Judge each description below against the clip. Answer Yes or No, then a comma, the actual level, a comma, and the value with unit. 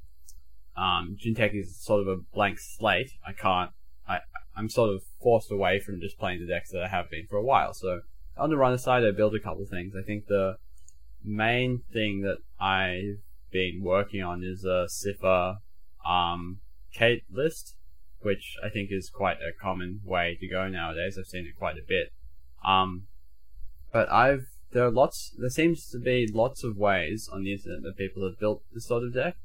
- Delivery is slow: No, average, 195 wpm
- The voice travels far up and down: No, average, 3.6 semitones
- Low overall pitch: Yes, very low, 95 Hz